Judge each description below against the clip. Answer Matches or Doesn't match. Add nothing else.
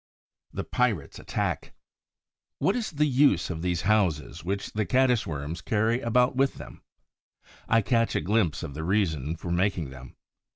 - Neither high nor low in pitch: Doesn't match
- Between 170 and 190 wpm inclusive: Doesn't match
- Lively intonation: Matches